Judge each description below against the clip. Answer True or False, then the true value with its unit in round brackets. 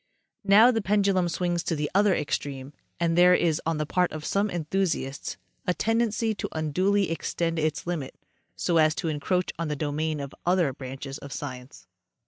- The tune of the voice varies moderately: True (4.0 semitones)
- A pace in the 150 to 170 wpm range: False (180 wpm)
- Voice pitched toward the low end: False (165 Hz)